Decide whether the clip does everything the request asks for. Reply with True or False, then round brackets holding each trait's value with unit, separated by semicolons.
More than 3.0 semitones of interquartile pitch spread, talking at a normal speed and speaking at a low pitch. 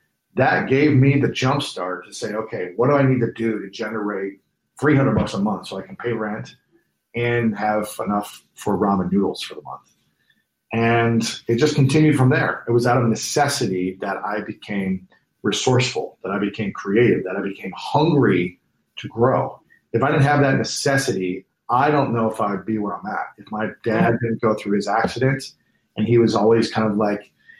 True (4.1 semitones; 195 wpm; 115 Hz)